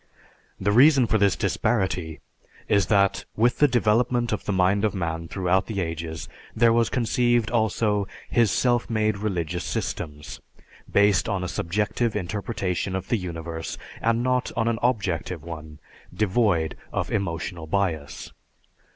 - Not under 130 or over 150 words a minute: Yes, average, 140 wpm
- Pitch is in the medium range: No, low, 100 Hz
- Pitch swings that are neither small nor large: Yes, average, 4.9 semitones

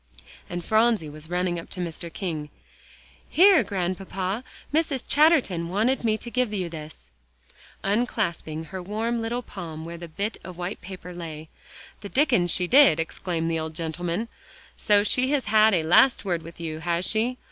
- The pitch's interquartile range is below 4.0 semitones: No, average, 5.1 semitones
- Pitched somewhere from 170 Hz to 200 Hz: Yes, medium, 185 Hz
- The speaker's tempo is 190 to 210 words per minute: No, average, 170 wpm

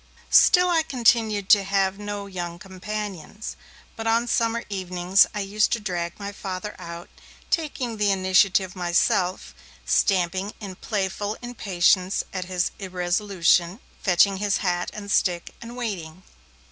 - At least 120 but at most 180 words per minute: Yes, slow, 135 wpm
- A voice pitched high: Yes, high, 195 Hz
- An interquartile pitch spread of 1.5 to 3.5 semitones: Yes, average, 2.7 semitones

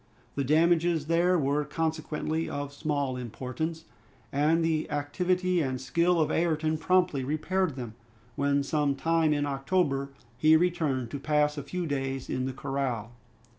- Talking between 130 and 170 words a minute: Yes, average, 145 wpm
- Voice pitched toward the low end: No, medium, 150 Hz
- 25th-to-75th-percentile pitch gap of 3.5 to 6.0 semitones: No, average, 3.1 semitones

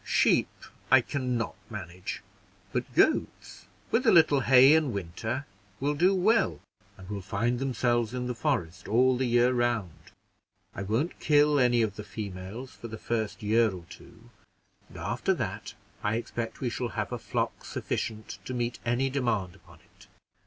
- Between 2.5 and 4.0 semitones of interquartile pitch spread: Yes, average, 3.6 semitones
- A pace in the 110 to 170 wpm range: Yes, average, 165 wpm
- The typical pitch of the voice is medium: No, low, 120 Hz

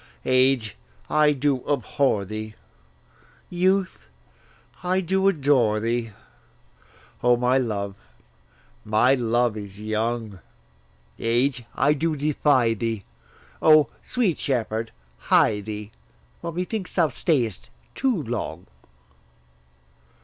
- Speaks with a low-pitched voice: Yes, low, 125 Hz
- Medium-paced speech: No, slow, 100 wpm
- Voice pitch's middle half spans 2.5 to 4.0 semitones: No, wide, 5.6 semitones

